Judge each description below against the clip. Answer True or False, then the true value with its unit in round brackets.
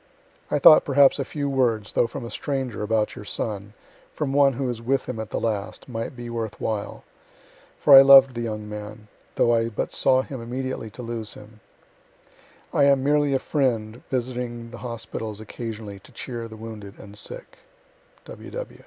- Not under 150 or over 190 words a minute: True (180 wpm)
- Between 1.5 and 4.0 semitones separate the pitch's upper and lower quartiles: True (3.5 semitones)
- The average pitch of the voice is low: True (115 Hz)